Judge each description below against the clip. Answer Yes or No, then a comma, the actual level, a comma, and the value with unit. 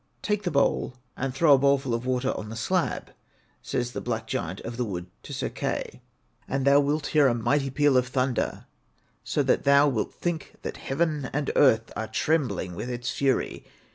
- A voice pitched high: No, low, 135 Hz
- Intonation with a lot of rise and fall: No, average, 3.2 semitones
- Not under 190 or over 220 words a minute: Yes, average, 195 wpm